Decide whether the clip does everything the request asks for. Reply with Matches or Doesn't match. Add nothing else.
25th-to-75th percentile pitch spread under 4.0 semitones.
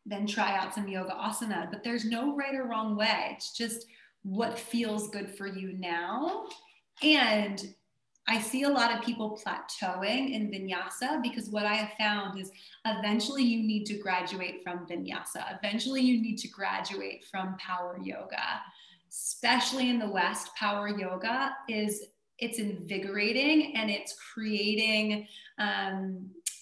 Matches